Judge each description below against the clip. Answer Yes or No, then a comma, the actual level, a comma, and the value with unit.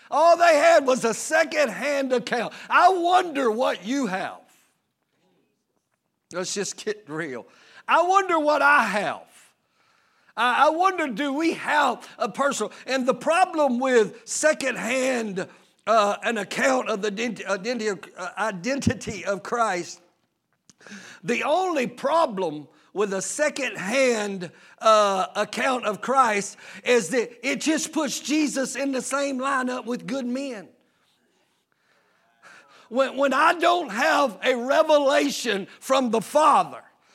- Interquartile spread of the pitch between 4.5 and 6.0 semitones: Yes, average, 5.3 semitones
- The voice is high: Yes, very high, 260 Hz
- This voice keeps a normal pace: No, slow, 120 wpm